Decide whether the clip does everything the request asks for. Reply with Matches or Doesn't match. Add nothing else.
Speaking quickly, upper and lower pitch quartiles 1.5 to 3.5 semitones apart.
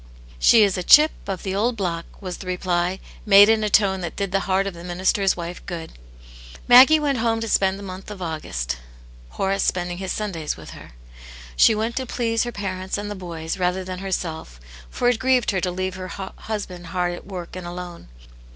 Matches